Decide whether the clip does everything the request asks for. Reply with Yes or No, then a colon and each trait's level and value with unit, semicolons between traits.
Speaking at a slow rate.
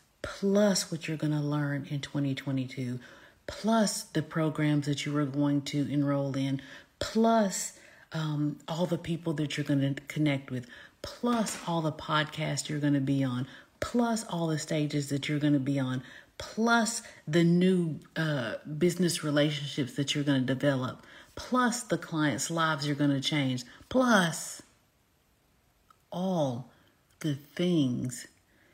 No: average, 150 wpm